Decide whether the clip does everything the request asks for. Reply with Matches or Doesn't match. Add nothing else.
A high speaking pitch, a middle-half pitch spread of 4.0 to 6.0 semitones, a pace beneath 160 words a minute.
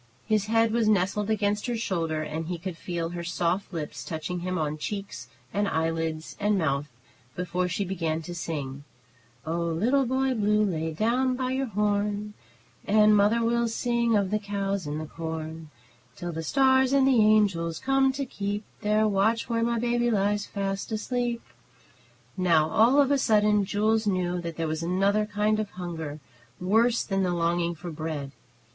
Doesn't match